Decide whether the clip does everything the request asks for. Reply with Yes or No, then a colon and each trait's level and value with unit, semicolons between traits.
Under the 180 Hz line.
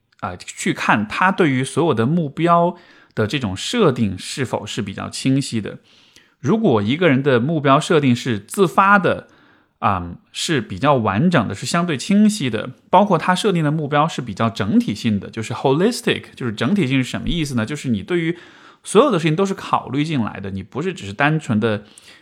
Yes: medium, 140 Hz